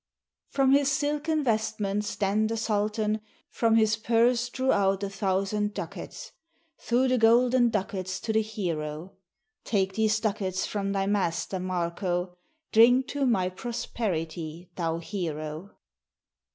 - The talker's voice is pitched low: No, high, 210 Hz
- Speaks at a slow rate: Yes, slow, 125 wpm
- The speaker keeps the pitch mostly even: No, average, 3.7 semitones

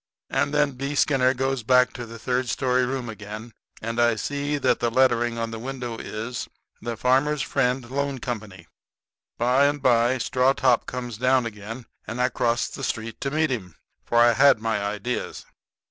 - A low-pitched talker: Yes, low, 125 Hz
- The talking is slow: No, average, 185 wpm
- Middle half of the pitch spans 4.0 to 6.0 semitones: No, narrow, 2.5 semitones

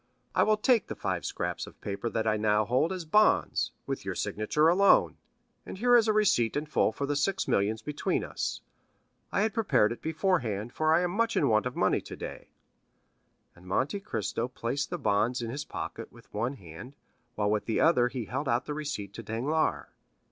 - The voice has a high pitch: No, low, 130 Hz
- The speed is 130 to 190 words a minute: No, average, 200 wpm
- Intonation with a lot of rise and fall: Yes, wide, 7.2 semitones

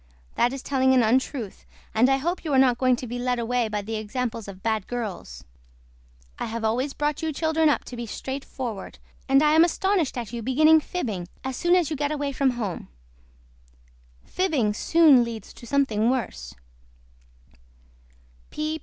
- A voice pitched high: Yes, very high, 255 Hz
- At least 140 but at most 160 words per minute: No, average, 170 wpm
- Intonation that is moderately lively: Yes, average, 4.3 semitones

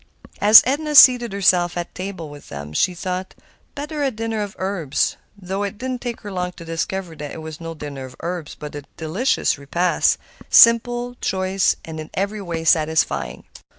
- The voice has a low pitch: No, medium, 185 Hz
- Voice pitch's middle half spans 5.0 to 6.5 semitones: Yes, average, 5.3 semitones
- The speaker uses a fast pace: No, average, 185 wpm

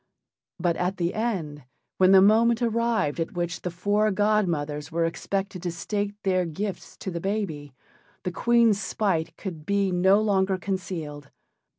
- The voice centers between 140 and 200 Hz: Yes, high, 190 Hz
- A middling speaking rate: Yes, average, 155 wpm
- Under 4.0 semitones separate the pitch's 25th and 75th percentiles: Yes, average, 3.5 semitones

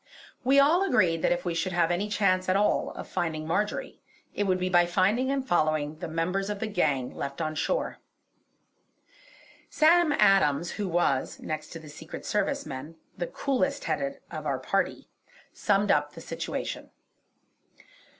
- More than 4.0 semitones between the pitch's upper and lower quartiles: Yes, average, 4.7 semitones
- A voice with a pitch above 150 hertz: Yes, medium, 185 Hz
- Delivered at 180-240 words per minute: No, average, 165 wpm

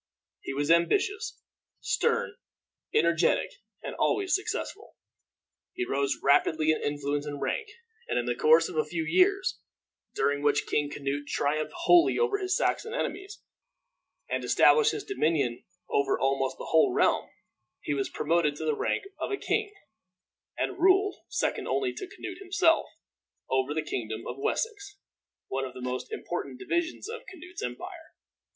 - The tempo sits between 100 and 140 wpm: No, average, 150 wpm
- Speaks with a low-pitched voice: No, medium, 165 Hz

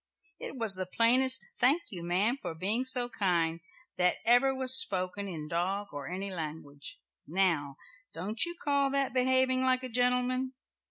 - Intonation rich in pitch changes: Yes, wide, 6.3 semitones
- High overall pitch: Yes, high, 220 Hz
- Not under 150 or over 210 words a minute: Yes, average, 160 wpm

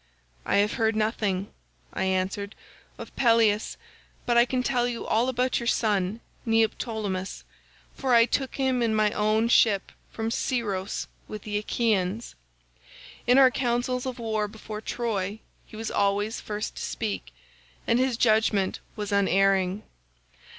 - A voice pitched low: No, high, 220 Hz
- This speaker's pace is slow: No, average, 145 wpm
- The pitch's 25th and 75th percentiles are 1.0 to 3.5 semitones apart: Yes, average, 2.8 semitones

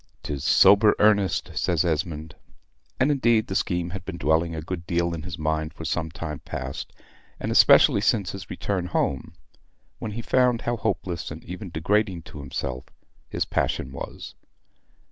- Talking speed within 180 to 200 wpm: No, average, 165 wpm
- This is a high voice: No, very low, 85 Hz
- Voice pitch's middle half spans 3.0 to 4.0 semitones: No, average, 4.4 semitones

